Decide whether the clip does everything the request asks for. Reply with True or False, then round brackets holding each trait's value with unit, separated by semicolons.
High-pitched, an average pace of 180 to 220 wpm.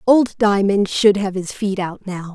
True (200 Hz; 205 wpm)